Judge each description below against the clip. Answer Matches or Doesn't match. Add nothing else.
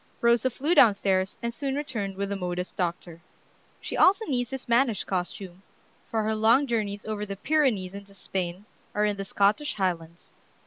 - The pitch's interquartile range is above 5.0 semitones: Doesn't match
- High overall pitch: Matches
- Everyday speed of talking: Matches